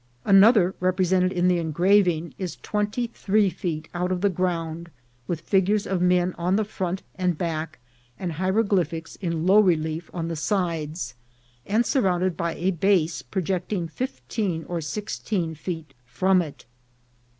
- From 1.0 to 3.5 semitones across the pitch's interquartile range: Yes, average, 2.7 semitones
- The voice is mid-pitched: Yes, medium, 180 Hz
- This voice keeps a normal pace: Yes, average, 150 wpm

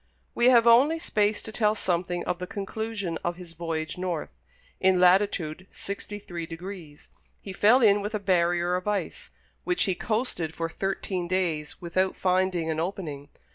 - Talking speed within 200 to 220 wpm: No, average, 165 wpm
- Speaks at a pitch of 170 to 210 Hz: Yes, medium, 185 Hz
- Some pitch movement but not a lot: Yes, average, 3.3 semitones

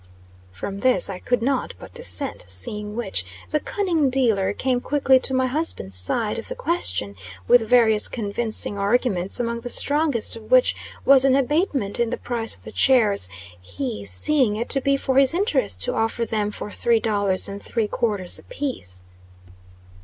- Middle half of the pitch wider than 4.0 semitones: Yes, average, 4.9 semitones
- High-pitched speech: Yes, high, 235 Hz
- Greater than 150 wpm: Yes, average, 175 wpm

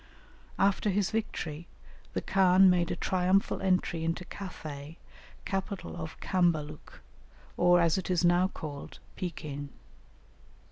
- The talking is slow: Yes, slow, 120 wpm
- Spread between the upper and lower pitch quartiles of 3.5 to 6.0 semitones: No, average, 2.8 semitones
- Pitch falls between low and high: Yes, medium, 175 Hz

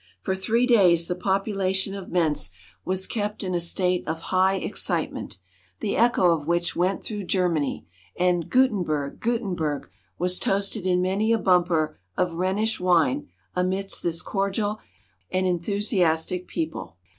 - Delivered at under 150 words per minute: Yes, average, 140 wpm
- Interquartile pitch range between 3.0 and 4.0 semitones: No, narrow, 2.5 semitones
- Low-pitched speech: No, medium, 185 Hz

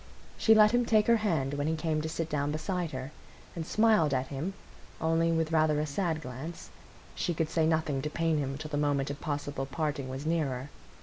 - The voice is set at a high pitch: No, medium, 155 Hz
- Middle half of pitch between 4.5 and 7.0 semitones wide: No, narrow, 2.6 semitones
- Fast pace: Yes, fast, 210 wpm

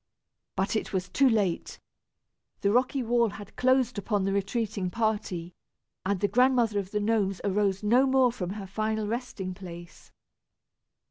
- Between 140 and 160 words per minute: Yes, average, 150 wpm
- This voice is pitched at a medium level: No, high, 210 Hz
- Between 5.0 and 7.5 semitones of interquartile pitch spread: No, average, 3.3 semitones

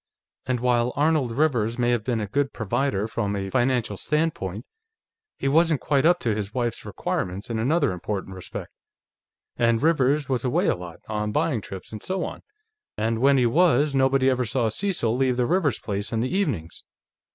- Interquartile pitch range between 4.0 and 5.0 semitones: Yes, average, 4.6 semitones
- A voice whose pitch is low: Yes, low, 120 Hz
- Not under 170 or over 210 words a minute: Yes, average, 185 wpm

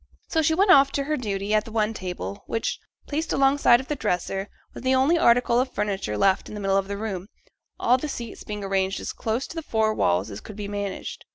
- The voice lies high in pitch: Yes, high, 215 Hz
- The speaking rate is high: Yes, fast, 240 wpm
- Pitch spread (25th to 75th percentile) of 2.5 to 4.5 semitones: No, average, 5.2 semitones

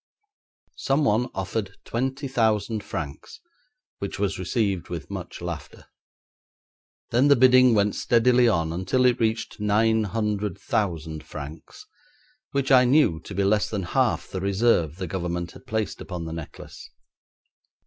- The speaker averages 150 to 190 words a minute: No, average, 140 wpm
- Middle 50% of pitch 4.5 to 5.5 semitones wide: Yes, average, 5.0 semitones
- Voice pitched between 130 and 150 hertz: No, low, 105 Hz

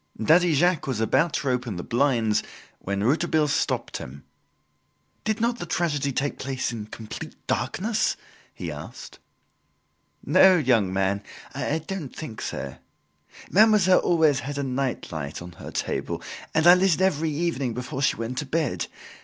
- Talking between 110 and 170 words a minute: Yes, average, 155 wpm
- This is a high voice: No, medium, 140 Hz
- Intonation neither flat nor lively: No, wide, 6.5 semitones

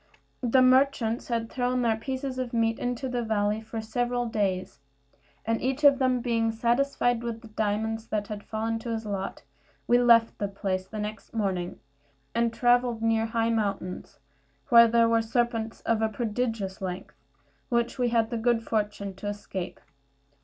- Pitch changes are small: Yes, narrow, 1.9 semitones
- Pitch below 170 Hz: No, high, 225 Hz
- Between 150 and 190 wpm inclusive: Yes, average, 165 wpm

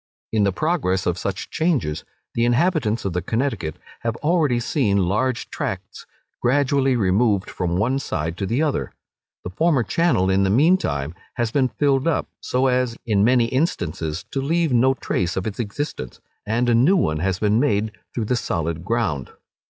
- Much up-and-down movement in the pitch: Yes, wide, 6.0 semitones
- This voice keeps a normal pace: Yes, average, 175 wpm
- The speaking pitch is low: Yes, low, 115 Hz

